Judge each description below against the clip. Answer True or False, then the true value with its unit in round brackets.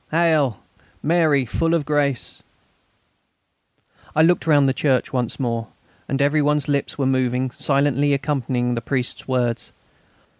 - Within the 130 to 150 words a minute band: True (135 wpm)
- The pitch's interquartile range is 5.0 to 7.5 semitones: False (2.7 semitones)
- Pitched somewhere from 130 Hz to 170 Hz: True (140 Hz)